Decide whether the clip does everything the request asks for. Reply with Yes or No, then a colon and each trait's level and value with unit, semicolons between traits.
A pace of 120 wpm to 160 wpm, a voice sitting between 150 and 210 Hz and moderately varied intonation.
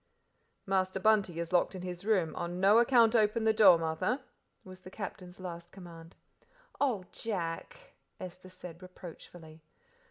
Yes: average, 140 wpm; medium, 185 Hz; average, 3.6 semitones